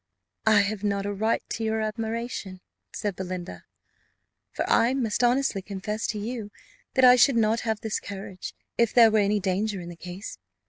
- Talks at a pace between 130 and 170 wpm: No, average, 180 wpm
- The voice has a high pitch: Yes, high, 215 Hz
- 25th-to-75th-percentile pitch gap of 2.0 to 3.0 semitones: Yes, narrow, 2.5 semitones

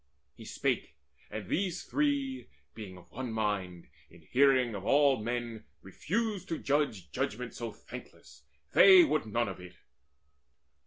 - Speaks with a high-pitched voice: No, low, 120 Hz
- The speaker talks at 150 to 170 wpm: No, average, 140 wpm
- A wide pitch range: Yes, wide, 7.8 semitones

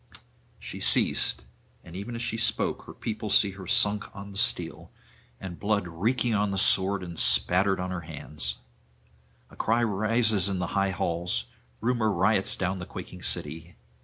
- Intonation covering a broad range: No, average, 3.3 semitones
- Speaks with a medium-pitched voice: No, very low, 95 Hz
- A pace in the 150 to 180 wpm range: Yes, average, 165 wpm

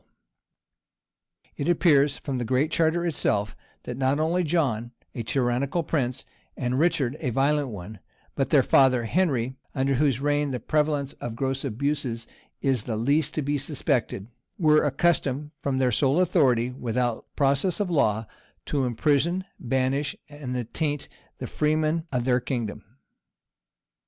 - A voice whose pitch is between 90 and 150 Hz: Yes, low, 135 Hz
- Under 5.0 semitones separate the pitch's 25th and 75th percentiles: Yes, average, 3.4 semitones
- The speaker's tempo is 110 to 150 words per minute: Yes, average, 145 wpm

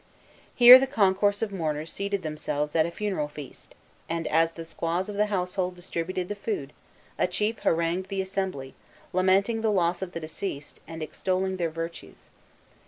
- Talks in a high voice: No, medium, 180 Hz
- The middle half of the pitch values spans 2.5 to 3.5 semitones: Yes, average, 3.2 semitones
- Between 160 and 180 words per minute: Yes, average, 170 wpm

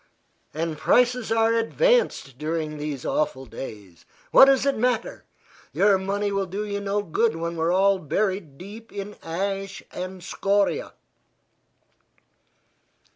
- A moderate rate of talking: No, slow, 130 wpm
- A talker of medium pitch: No, high, 195 Hz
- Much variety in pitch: No, average, 4.8 semitones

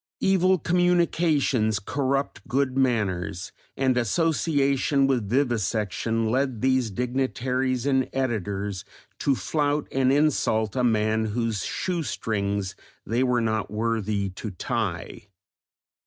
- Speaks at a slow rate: Yes, slow, 110 wpm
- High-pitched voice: No, low, 125 Hz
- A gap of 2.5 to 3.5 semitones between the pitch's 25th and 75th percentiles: No, average, 4.1 semitones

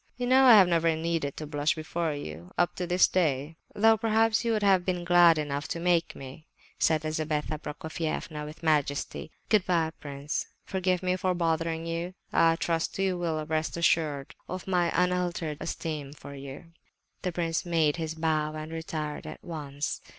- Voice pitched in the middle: Yes, medium, 165 Hz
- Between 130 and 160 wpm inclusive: No, average, 170 wpm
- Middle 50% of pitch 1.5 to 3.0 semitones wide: Yes, narrow, 2.6 semitones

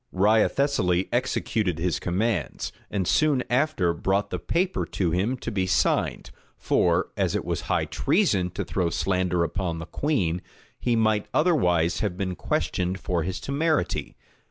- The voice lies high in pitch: No, very low, 95 Hz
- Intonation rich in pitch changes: Yes, wide, 5.7 semitones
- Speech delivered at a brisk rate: No, average, 150 wpm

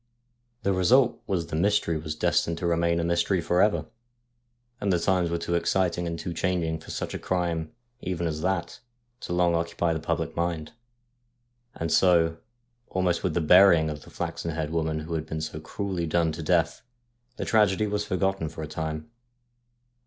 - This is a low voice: Yes, very low, 85 Hz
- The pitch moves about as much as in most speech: No, narrow, 2.3 semitones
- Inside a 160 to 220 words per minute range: Yes, average, 180 wpm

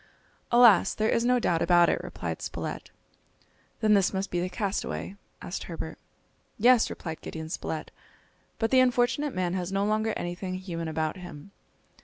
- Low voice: No, high, 190 Hz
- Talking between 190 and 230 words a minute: No, average, 160 wpm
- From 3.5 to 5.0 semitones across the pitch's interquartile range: Yes, average, 4.2 semitones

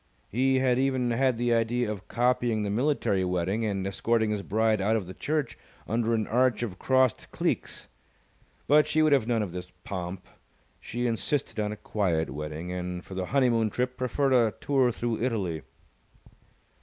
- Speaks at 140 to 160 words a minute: No, average, 175 wpm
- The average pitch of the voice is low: Yes, low, 115 Hz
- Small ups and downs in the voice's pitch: No, average, 4.3 semitones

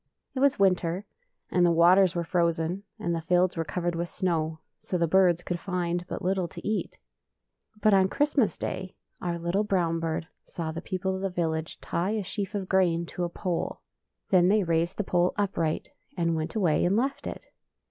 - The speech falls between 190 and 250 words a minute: Yes, average, 195 wpm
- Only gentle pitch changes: Yes, narrow, 2.2 semitones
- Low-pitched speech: No, medium, 175 Hz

